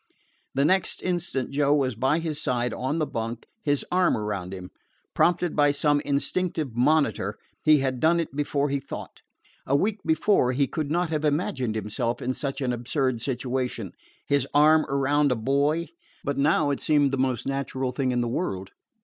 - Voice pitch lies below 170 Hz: Yes, medium, 140 Hz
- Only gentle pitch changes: No, average, 3.3 semitones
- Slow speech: No, average, 180 wpm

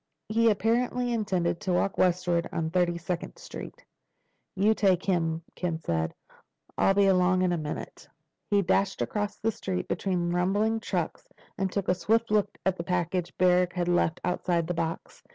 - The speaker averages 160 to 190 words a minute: Yes, average, 170 wpm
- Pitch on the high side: No, medium, 180 Hz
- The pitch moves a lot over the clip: No, average, 2.7 semitones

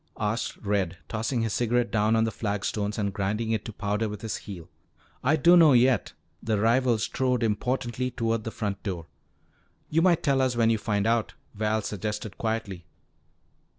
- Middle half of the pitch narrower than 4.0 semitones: Yes, narrow, 2.6 semitones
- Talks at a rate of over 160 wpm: Yes, average, 170 wpm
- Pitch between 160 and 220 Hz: No, low, 110 Hz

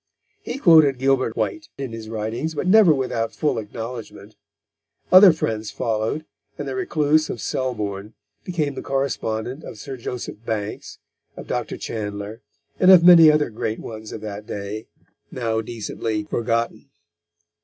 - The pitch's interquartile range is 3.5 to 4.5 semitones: No, wide, 5.6 semitones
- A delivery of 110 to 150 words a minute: Yes, average, 145 wpm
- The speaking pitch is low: Yes, low, 115 Hz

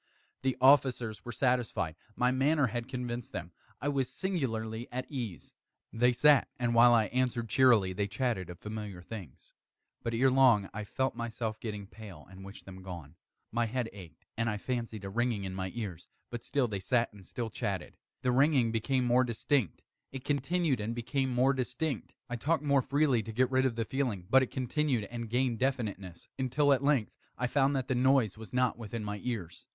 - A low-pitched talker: Yes, low, 120 Hz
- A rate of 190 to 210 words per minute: Yes, average, 195 wpm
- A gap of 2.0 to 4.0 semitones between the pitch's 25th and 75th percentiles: Yes, average, 3.6 semitones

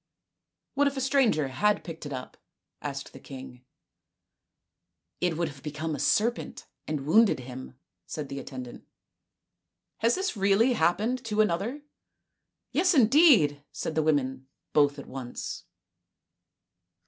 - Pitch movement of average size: No, wide, 8.6 semitones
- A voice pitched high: No, medium, 160 Hz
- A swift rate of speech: No, average, 150 wpm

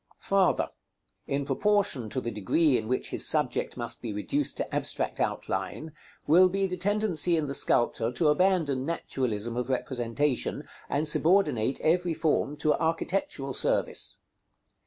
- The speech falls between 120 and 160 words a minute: Yes, average, 150 wpm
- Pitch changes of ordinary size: No, wide, 6.0 semitones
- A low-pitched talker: No, medium, 150 Hz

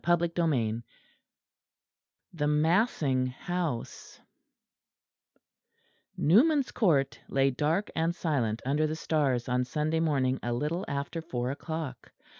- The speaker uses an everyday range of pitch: Yes, average, 4.4 semitones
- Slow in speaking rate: Yes, slow, 105 wpm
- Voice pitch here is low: No, medium, 150 Hz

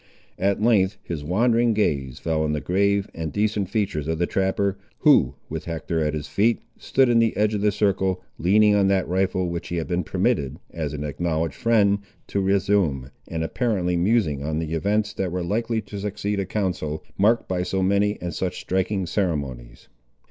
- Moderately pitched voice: No, very low, 95 Hz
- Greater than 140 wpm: Yes, average, 190 wpm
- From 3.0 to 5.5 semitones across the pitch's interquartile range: Yes, average, 4.1 semitones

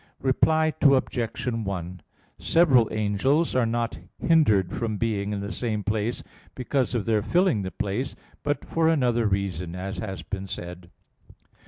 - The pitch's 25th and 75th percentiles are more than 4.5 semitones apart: Yes, average, 4.9 semitones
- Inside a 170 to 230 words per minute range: No, average, 145 wpm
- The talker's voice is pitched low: Yes, low, 110 Hz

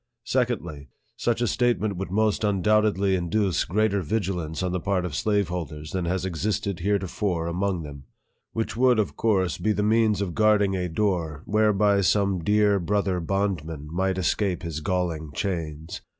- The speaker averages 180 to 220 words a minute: No, average, 165 wpm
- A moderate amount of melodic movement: Yes, average, 3.6 semitones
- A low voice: Yes, very low, 95 Hz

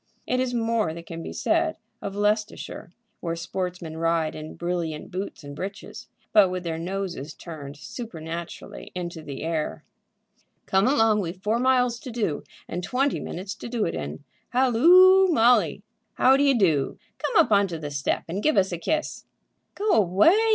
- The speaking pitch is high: Yes, high, 195 Hz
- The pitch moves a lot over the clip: Yes, wide, 6.5 semitones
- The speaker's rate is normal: Yes, average, 170 wpm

